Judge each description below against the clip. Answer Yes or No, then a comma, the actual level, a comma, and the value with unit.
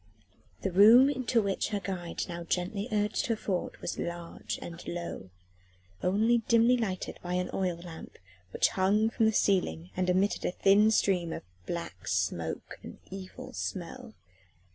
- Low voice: No, high, 190 Hz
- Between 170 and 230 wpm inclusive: No, average, 155 wpm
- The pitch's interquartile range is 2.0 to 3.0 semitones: No, average, 3.9 semitones